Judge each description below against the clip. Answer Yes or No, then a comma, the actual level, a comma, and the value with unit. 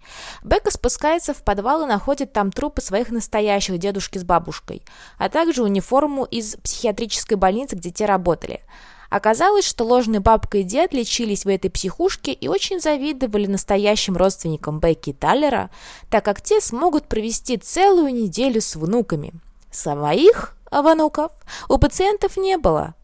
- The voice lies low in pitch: No, high, 230 Hz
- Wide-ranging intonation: Yes, wide, 7.3 semitones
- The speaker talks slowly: No, average, 145 wpm